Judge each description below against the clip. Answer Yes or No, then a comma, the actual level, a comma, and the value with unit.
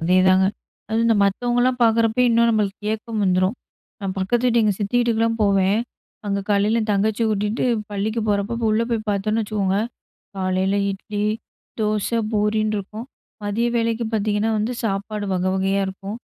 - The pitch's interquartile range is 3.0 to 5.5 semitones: No, narrow, 2.4 semitones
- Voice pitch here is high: Yes, high, 210 Hz